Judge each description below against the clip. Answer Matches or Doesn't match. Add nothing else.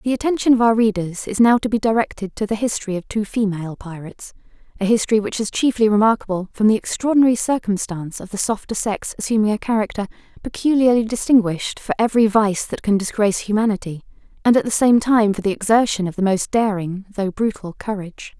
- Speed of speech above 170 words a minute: Matches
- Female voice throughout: Matches